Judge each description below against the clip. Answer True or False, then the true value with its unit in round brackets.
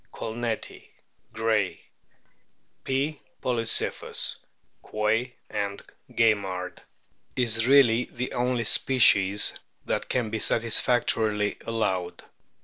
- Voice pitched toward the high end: False (115 Hz)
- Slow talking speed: True (80 wpm)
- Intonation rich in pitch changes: False (2.7 semitones)